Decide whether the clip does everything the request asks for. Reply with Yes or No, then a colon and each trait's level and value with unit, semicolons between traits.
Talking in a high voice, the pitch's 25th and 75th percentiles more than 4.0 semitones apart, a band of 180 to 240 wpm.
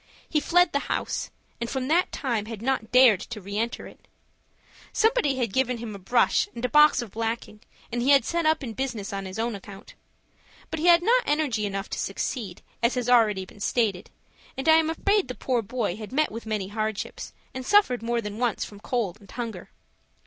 Yes: high, 235 Hz; average, 4.5 semitones; fast, 205 wpm